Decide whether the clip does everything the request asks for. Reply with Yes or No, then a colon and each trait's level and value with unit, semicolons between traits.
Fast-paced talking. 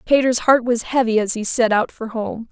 Yes: fast, 240 wpm